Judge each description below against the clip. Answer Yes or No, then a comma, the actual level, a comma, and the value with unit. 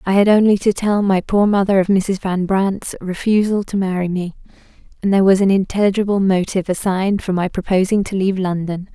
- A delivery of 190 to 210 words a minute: Yes, average, 195 wpm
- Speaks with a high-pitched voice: Yes, high, 195 Hz